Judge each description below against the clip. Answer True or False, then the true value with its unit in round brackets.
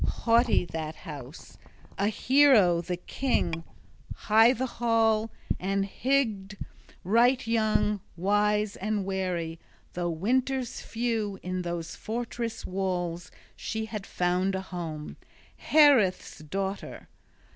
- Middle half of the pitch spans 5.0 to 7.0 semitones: False (4.3 semitones)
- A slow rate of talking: True (110 wpm)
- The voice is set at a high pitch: True (200 Hz)